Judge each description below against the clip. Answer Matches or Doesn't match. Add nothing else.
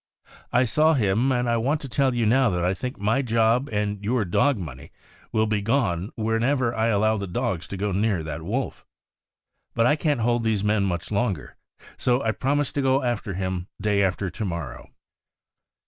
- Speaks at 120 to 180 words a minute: Doesn't match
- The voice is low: Matches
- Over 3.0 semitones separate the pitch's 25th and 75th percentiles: Matches